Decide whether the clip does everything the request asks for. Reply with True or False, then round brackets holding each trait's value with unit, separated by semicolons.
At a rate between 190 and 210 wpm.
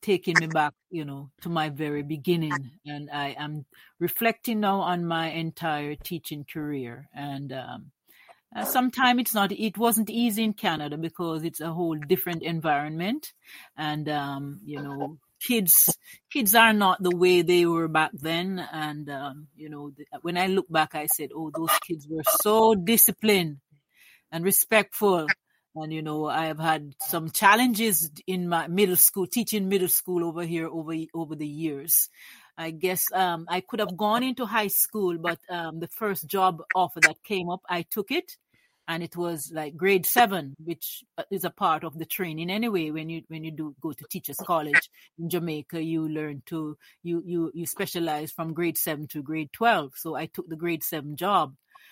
False (180 wpm)